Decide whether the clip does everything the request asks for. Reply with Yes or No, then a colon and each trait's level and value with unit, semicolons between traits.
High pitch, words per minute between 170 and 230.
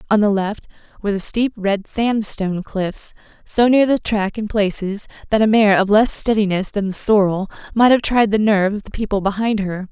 Yes: high, 205 Hz; fast, 205 wpm